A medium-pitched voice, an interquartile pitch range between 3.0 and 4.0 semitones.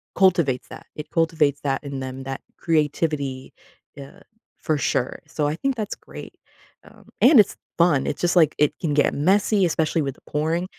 Yes: medium, 155 Hz; average, 3.6 semitones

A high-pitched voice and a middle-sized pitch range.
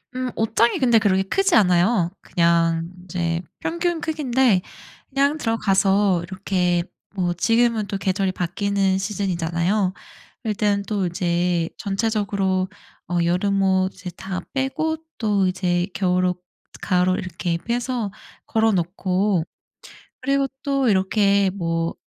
Yes: high, 195 Hz; average, 3.7 semitones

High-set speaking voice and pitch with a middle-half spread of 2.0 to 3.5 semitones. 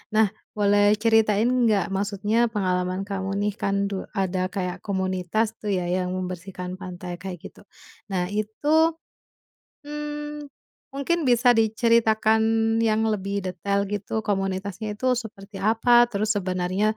Yes: high, 205 Hz; average, 2.9 semitones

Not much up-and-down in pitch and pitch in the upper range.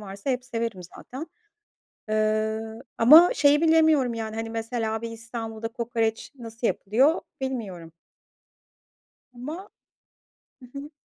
No: average, 3.1 semitones; high, 230 Hz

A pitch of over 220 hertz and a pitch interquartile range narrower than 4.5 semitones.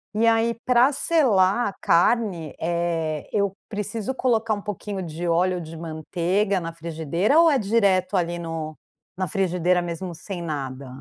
No: medium, 185 Hz; average, 4.1 semitones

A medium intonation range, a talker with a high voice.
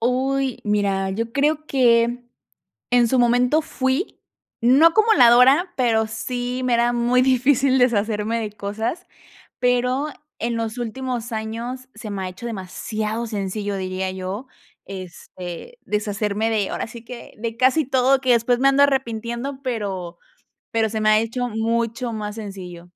Yes: average, 3.1 semitones; high, 235 Hz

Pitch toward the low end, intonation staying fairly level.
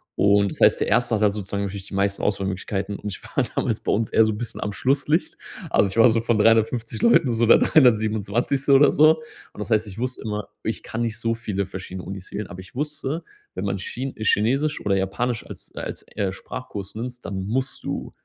No: low, 110 Hz; average, 3.7 semitones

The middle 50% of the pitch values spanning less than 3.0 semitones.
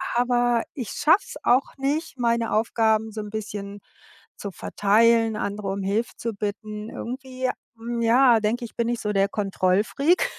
Yes: narrow, 2.6 semitones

